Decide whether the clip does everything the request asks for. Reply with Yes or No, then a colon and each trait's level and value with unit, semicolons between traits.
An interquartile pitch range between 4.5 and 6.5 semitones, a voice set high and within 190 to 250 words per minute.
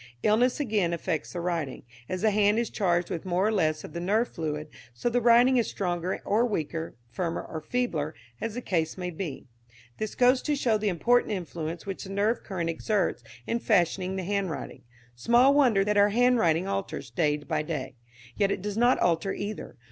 Yes: average, 4.9 semitones; high, 195 Hz; average, 195 wpm